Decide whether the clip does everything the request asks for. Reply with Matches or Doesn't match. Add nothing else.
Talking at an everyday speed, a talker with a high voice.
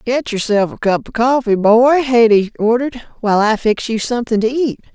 Matches